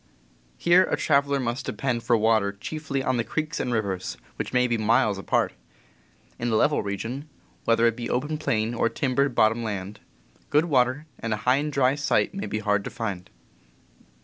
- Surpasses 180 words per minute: Yes, average, 190 wpm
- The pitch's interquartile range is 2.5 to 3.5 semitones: No, average, 4.3 semitones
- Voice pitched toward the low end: Yes, low, 120 Hz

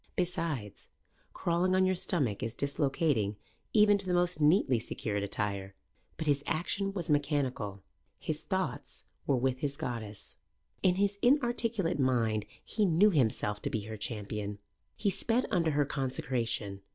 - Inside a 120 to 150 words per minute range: Yes, average, 145 wpm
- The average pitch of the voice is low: No, medium, 145 Hz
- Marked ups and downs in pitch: Yes, wide, 8.6 semitones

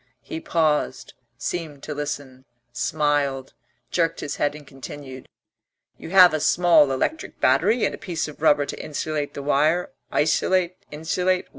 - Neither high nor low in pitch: Yes, medium, 150 Hz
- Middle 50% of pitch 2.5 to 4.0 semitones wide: Yes, average, 3.4 semitones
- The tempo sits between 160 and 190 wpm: No, average, 145 wpm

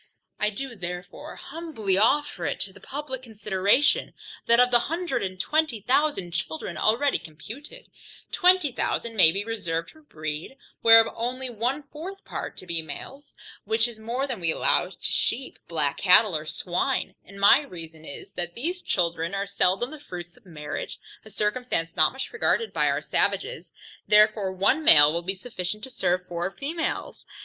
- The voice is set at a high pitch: Yes, high, 215 Hz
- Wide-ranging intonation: Yes, wide, 7.2 semitones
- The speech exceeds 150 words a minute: Yes, average, 170 wpm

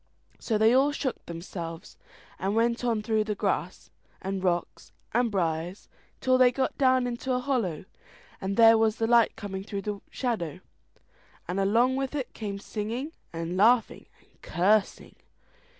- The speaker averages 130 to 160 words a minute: Yes, average, 150 wpm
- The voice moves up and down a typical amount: Yes, average, 4.3 semitones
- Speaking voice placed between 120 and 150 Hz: No, high, 220 Hz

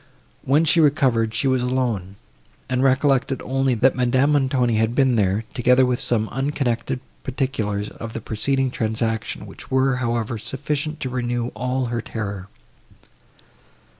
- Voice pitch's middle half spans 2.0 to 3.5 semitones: Yes, average, 2.7 semitones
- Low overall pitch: Yes, low, 125 Hz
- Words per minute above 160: No, average, 140 wpm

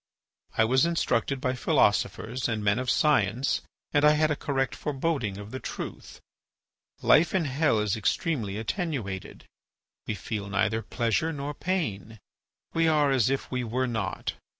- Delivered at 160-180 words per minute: No, average, 150 wpm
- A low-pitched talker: Yes, low, 130 Hz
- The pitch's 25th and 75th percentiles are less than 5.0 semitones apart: No, wide, 5.4 semitones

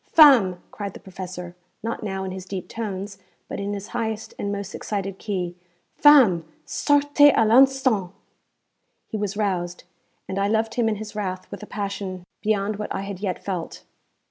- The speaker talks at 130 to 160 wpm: No, average, 170 wpm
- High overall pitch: Yes, high, 200 Hz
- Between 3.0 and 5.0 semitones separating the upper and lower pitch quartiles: No, narrow, 2.6 semitones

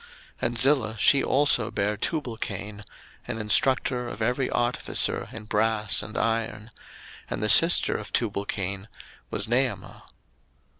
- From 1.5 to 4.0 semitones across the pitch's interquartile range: Yes, average, 2.8 semitones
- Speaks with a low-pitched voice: Yes, low, 115 Hz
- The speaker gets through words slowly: Yes, slow, 130 wpm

